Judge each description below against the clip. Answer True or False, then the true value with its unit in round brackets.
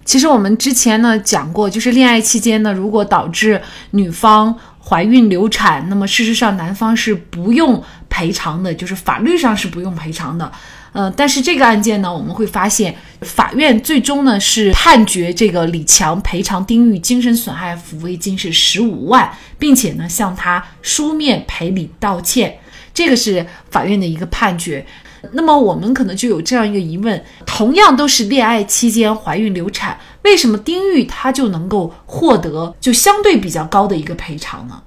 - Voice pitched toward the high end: True (215 Hz)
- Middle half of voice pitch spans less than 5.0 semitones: True (4.6 semitones)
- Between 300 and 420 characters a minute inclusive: False (275 characters per minute)